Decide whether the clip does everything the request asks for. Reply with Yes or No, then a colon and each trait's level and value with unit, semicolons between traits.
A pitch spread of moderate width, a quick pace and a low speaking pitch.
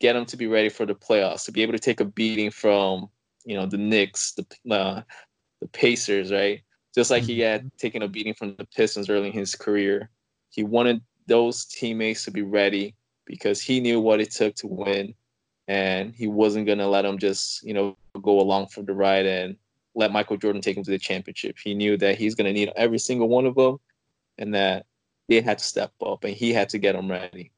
No: narrow, 2.3 semitones; fast, 220 wpm; low, 105 Hz